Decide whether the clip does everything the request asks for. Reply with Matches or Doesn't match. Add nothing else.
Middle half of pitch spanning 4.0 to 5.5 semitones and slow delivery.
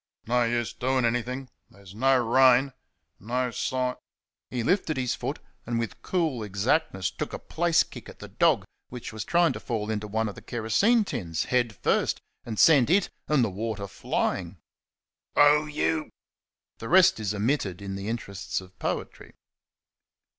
Doesn't match